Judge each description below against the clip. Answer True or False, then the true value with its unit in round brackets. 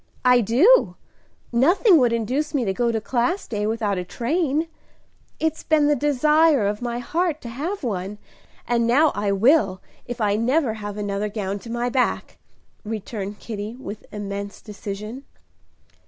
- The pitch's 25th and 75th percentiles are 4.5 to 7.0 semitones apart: True (5.6 semitones)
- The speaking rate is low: False (155 wpm)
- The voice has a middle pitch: False (235 Hz)